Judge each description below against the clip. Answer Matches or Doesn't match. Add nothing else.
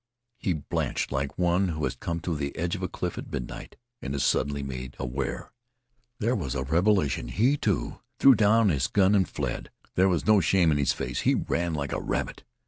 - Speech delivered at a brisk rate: Matches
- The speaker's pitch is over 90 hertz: Doesn't match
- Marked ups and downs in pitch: Matches